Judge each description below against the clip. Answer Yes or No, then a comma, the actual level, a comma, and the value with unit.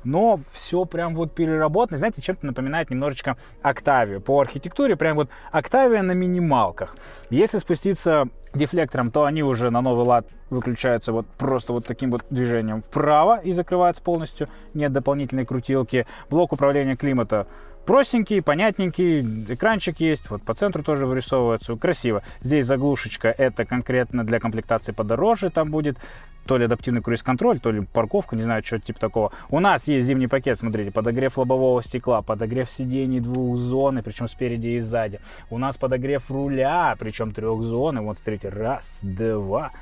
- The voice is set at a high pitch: No, low, 130 Hz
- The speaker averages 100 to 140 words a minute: No, average, 155 wpm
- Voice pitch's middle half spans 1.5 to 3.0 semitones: No, average, 4.7 semitones